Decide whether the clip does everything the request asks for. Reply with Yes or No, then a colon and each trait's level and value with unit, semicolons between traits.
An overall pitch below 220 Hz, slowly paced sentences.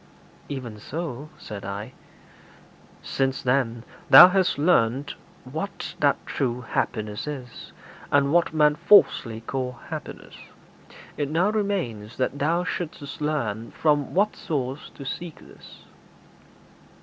Yes: medium, 140 Hz; slow, 115 wpm